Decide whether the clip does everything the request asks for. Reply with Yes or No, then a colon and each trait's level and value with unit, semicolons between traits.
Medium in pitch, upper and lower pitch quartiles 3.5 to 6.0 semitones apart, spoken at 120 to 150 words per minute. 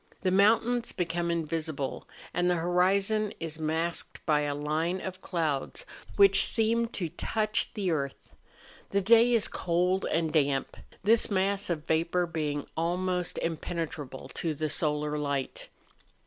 Yes: medium, 170 Hz; average, 4.0 semitones; average, 140 wpm